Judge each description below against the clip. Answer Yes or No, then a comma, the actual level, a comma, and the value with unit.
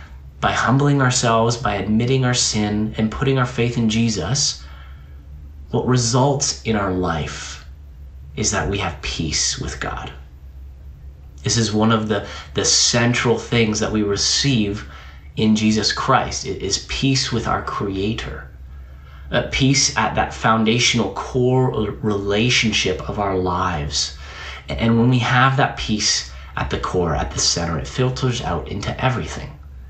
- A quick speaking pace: No, average, 145 wpm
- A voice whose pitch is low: Yes, low, 105 Hz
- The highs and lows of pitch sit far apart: Yes, wide, 8.7 semitones